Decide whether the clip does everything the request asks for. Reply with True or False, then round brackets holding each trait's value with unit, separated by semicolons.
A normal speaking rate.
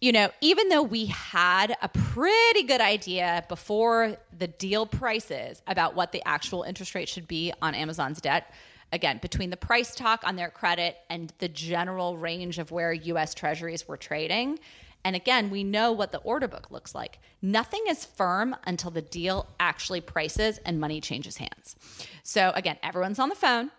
True (180 wpm)